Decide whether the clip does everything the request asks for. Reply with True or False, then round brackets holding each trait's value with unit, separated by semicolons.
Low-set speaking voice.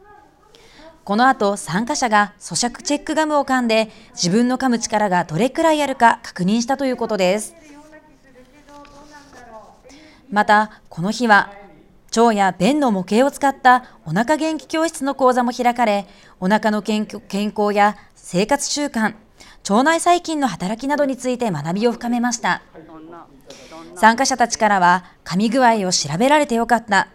False (235 Hz)